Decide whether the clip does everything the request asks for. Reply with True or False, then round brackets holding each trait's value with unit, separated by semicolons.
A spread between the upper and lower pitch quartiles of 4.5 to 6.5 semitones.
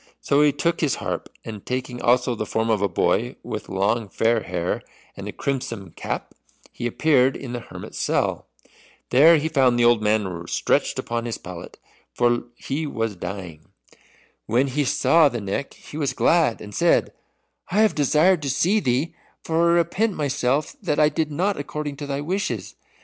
True (5.2 semitones)